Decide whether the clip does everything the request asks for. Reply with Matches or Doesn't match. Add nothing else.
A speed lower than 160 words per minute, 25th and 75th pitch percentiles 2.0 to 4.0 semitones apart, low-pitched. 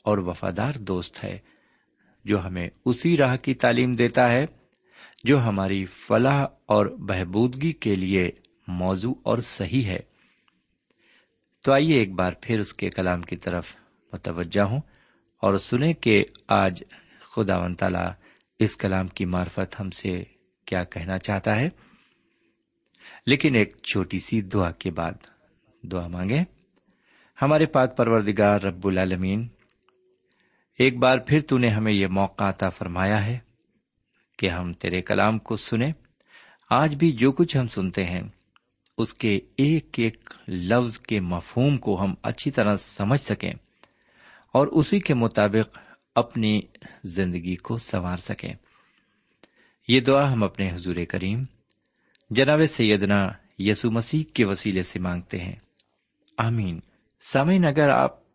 Doesn't match